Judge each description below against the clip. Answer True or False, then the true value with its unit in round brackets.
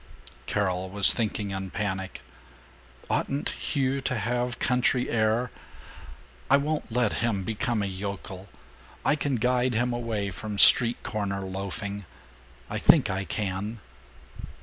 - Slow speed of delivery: True (125 wpm)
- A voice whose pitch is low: True (110 Hz)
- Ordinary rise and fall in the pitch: True (3.9 semitones)